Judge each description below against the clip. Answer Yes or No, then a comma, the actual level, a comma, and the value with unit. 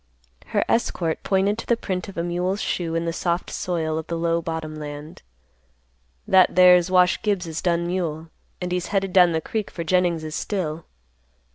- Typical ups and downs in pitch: No, narrow, 2.2 semitones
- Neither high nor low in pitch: Yes, medium, 175 Hz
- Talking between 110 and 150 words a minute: No, average, 175 wpm